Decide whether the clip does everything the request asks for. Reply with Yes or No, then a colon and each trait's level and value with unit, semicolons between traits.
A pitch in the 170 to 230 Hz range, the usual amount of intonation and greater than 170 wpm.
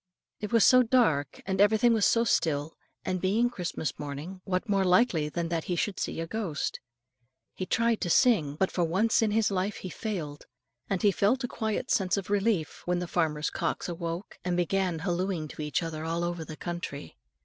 Yes: medium, 185 Hz; average, 4.2 semitones; average, 200 wpm